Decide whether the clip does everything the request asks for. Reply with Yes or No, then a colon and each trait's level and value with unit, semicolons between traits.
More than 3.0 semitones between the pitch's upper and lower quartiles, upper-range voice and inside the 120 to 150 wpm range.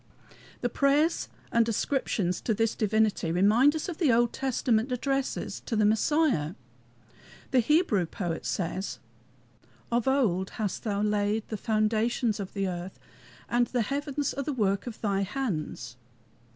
Yes: average, 5.0 semitones; high, 220 Hz; average, 145 wpm